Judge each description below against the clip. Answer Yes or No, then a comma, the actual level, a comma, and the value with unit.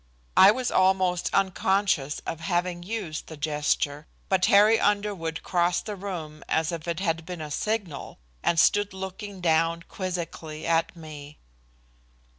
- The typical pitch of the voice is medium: Yes, medium, 175 Hz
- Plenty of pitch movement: No, average, 3.4 semitones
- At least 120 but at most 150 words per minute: Yes, average, 140 wpm